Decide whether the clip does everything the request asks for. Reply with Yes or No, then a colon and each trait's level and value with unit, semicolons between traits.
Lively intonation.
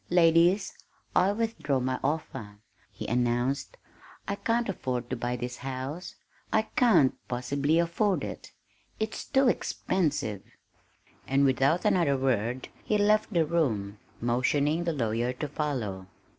Yes: wide, 6.2 semitones